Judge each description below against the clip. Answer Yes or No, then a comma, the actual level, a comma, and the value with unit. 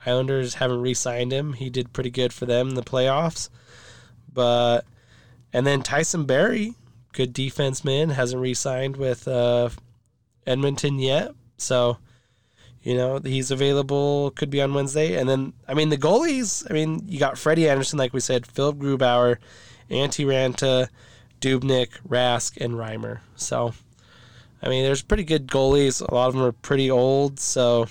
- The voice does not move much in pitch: Yes, narrow, 2.3 semitones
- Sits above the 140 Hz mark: No, low, 130 Hz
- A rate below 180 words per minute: Yes, average, 155 wpm